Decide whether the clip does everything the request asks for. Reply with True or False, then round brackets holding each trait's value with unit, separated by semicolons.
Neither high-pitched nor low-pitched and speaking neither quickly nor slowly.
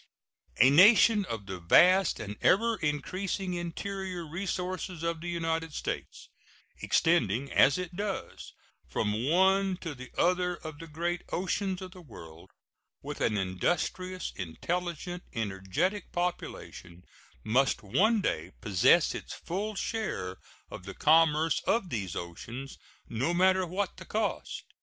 False (170 Hz; 130 wpm)